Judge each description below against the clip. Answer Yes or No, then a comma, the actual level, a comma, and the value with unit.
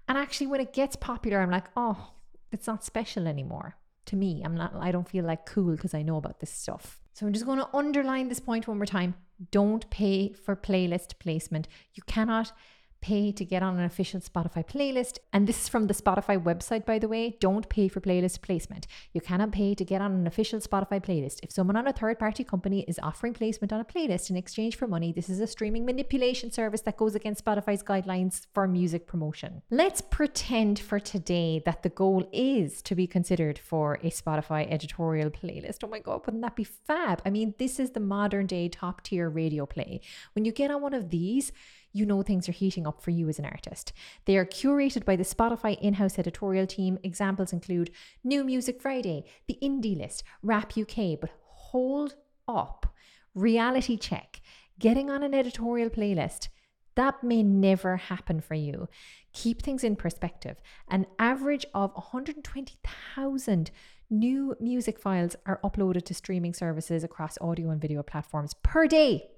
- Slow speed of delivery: No, average, 190 wpm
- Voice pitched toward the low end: No, high, 200 Hz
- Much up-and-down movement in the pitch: No, average, 4.6 semitones